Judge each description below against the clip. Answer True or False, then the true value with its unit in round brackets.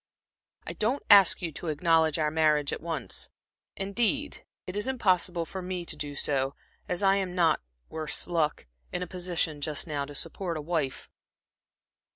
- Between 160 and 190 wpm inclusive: True (170 wpm)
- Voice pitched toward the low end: False (170 Hz)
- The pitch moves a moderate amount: True (3.6 semitones)